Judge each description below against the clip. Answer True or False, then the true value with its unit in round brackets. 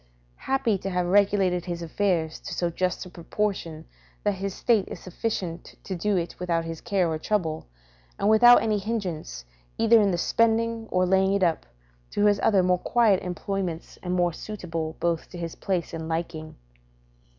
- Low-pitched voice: False (185 Hz)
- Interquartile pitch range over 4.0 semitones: False (3.4 semitones)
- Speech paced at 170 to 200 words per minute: True (175 wpm)